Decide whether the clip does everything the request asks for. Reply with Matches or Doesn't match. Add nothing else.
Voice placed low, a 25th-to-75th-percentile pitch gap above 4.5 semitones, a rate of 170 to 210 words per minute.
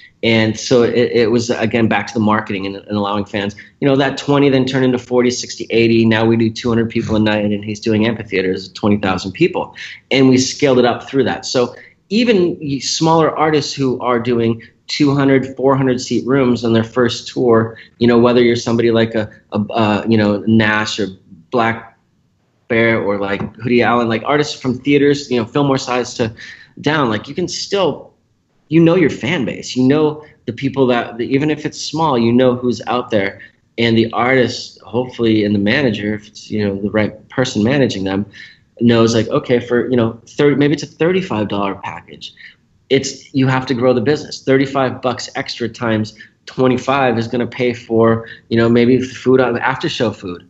Doesn't match